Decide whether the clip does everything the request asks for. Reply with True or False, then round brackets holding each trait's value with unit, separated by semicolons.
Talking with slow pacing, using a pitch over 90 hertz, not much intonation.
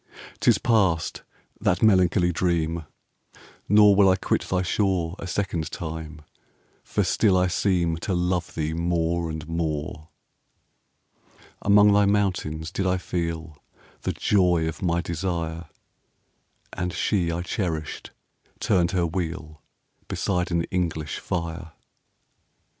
False (125 wpm; 85 Hz; 2.3 semitones)